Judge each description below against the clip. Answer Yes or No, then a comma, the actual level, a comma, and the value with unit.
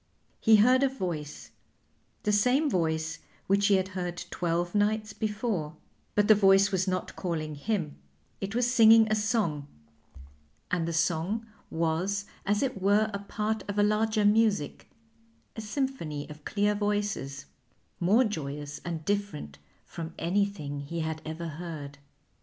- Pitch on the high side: Yes, high, 195 Hz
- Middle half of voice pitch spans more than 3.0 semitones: Yes, average, 4.7 semitones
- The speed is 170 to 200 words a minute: No, average, 145 wpm